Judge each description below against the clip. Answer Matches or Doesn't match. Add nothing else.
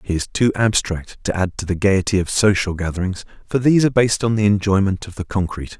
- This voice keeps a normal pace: Doesn't match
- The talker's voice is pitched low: Matches